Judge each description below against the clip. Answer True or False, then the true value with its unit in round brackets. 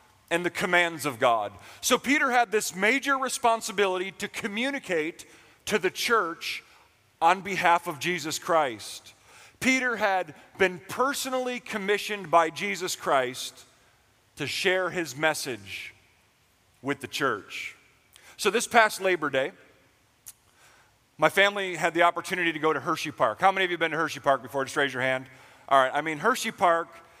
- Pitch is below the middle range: False (170 Hz)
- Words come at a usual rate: True (155 wpm)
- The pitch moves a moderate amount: False (6.5 semitones)